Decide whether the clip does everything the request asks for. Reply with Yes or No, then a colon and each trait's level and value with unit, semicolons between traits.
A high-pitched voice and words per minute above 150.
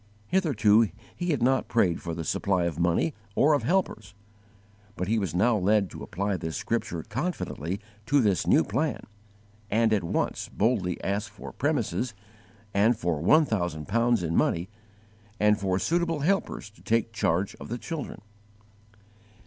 No: low, 105 Hz; average, 160 wpm